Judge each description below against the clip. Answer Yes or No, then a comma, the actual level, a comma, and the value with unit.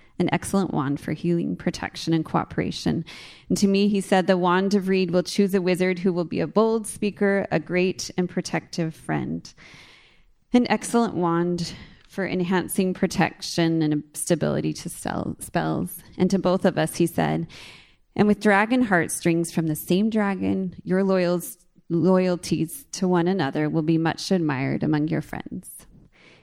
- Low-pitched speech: No, medium, 180 Hz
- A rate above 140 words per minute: Yes, average, 155 wpm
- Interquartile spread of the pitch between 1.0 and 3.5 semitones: Yes, average, 2.9 semitones